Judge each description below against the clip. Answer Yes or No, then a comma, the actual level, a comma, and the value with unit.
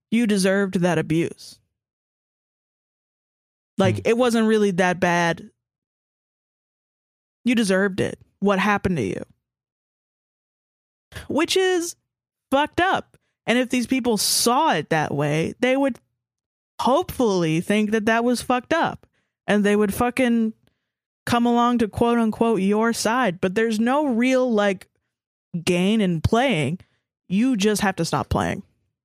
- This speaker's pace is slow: Yes, slow, 130 wpm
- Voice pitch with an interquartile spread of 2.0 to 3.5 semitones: No, average, 5.1 semitones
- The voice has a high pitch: Yes, high, 215 Hz